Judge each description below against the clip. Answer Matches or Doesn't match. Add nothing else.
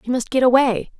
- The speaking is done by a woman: Matches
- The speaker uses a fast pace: Matches